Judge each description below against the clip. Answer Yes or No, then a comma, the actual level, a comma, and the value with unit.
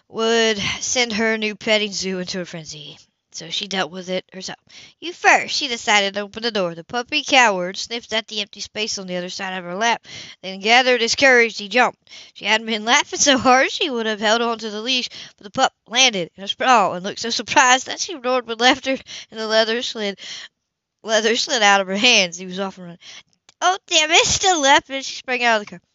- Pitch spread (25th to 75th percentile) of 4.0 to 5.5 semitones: Yes, average, 4.3 semitones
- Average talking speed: No, fast, 235 wpm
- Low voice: No, high, 225 Hz